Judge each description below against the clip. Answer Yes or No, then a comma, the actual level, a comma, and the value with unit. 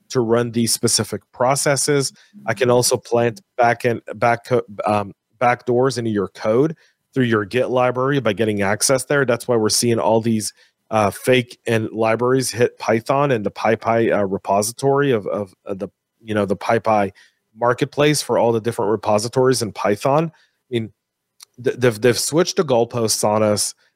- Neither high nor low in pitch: No, low, 115 Hz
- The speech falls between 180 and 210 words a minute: No, average, 170 wpm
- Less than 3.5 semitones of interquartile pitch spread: Yes, average, 2.9 semitones